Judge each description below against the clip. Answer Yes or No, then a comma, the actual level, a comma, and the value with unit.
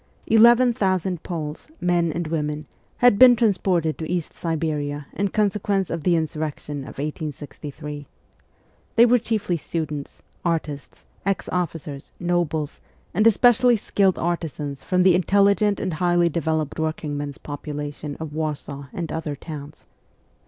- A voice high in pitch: No, medium, 165 Hz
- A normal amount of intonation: Yes, average, 4.2 semitones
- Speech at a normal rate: No, slow, 130 wpm